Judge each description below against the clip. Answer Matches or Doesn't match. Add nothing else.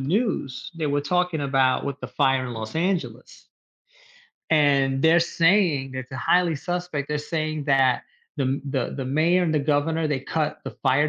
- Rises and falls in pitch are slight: Doesn't match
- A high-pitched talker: Doesn't match